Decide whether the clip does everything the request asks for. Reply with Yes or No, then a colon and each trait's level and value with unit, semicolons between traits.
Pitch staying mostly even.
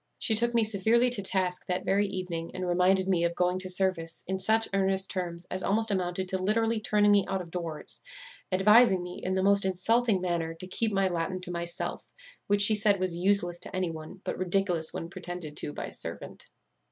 Yes: narrow, 2.3 semitones